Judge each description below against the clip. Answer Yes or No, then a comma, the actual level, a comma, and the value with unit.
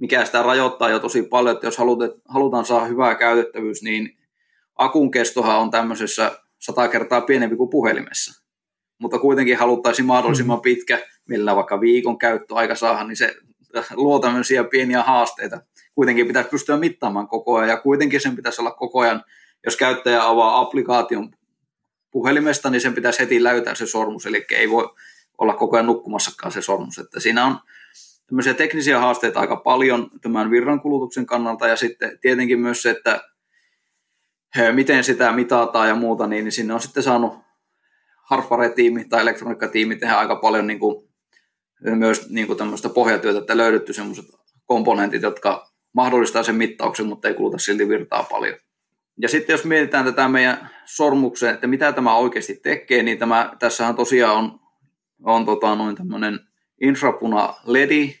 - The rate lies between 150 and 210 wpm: Yes, fast, 155 wpm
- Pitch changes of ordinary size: No, narrow, 2.3 semitones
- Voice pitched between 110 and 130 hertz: Yes, low, 120 Hz